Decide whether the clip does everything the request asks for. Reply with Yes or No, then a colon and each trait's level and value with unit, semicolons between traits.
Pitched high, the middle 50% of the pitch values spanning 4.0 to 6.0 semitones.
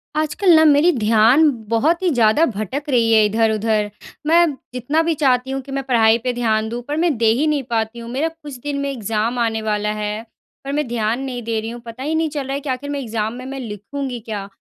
Yes: high, 245 Hz; average, 4.4 semitones